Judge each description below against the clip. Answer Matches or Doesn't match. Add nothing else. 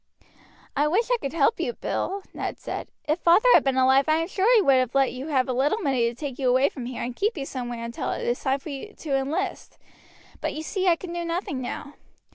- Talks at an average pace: Doesn't match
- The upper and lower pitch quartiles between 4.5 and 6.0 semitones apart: Matches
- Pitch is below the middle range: Doesn't match